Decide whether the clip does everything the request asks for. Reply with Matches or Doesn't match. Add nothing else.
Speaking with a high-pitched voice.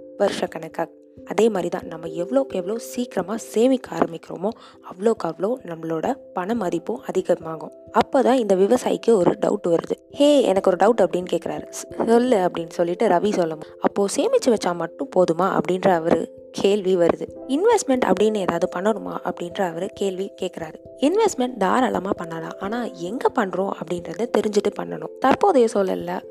Matches